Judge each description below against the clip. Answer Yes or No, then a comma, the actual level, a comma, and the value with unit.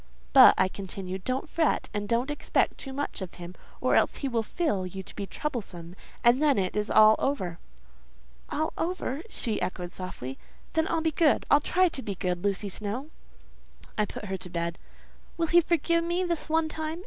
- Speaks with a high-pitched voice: Yes, high, 240 Hz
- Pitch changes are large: Yes, wide, 8.8 semitones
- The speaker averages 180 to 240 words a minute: Yes, average, 195 wpm